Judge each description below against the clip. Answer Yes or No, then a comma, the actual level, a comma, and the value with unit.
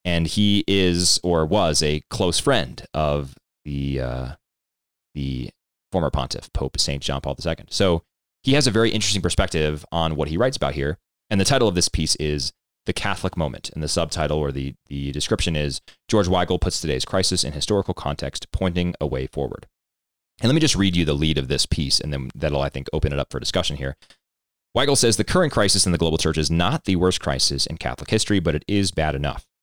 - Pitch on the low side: Yes, very low, 80 Hz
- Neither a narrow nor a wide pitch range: Yes, average, 4.8 semitones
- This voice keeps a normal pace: No, fast, 215 wpm